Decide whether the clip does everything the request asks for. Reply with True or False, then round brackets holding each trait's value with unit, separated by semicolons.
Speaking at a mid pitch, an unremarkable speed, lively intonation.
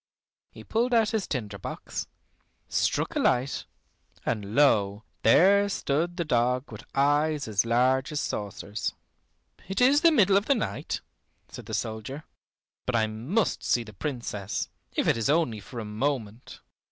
False (130 Hz; 155 wpm; 7.7 semitones)